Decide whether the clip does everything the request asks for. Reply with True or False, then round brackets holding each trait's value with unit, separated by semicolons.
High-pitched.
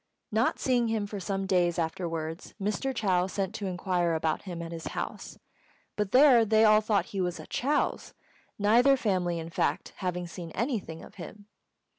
True (195 Hz)